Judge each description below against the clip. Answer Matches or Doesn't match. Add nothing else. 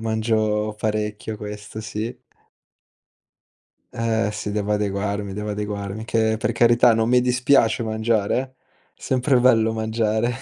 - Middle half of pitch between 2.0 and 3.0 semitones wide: Doesn't match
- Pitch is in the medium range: Doesn't match